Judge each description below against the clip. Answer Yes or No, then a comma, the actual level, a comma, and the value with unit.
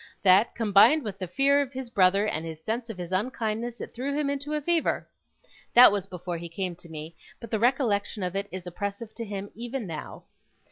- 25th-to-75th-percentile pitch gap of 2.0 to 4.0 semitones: No, average, 5.1 semitones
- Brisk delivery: Yes, fast, 215 wpm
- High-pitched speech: Yes, high, 210 Hz